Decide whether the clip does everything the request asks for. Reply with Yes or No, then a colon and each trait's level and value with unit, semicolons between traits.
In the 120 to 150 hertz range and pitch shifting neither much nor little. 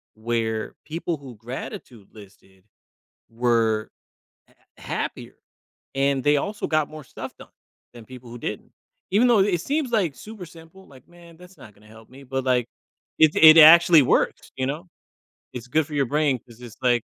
No: low, 135 Hz; wide, 5.7 semitones